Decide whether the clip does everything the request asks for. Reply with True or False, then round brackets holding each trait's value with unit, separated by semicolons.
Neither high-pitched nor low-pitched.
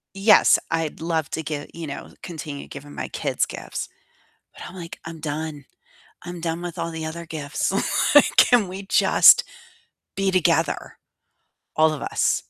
True (165 Hz)